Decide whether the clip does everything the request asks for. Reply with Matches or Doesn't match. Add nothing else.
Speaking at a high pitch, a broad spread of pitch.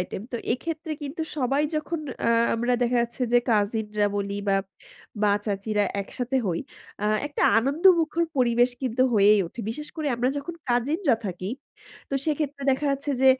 Matches